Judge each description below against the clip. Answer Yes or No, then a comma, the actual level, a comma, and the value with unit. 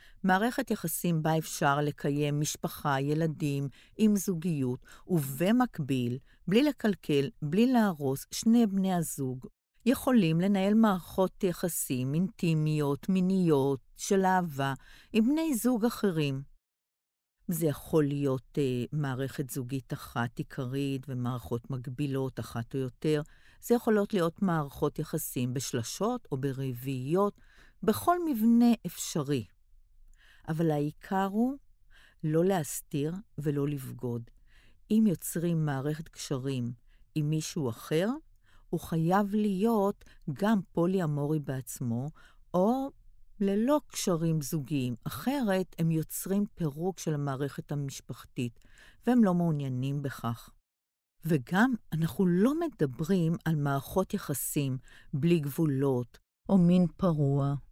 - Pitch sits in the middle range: Yes, medium, 155 Hz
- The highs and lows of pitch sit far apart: Yes, wide, 5.9 semitones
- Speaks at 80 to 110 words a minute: Yes, average, 105 wpm